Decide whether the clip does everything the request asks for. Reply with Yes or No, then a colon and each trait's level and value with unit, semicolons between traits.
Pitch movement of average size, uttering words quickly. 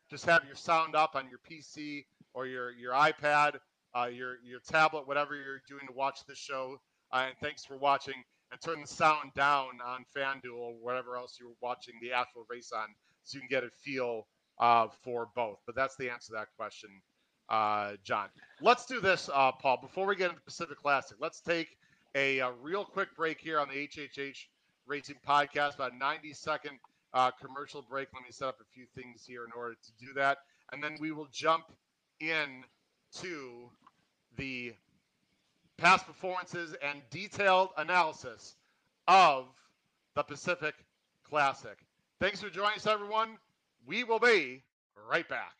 No: average, 3.9 semitones; average, 175 wpm